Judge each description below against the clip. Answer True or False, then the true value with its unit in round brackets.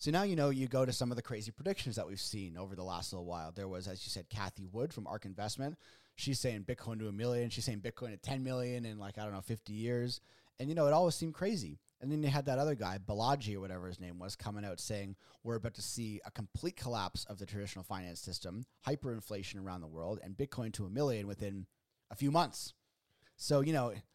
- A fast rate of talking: True (250 wpm)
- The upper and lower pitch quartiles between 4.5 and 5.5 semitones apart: True (4.9 semitones)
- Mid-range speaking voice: False (110 Hz)